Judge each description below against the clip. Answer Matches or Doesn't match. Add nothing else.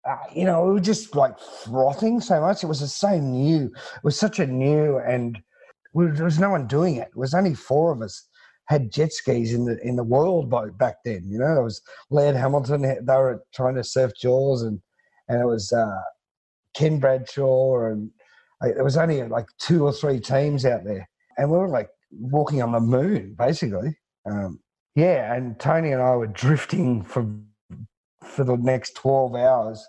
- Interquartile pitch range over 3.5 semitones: Matches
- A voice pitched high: Doesn't match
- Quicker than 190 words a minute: Matches